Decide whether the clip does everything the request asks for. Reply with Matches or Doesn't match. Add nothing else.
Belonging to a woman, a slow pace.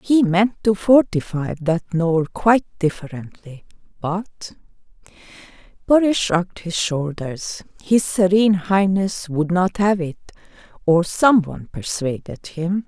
Matches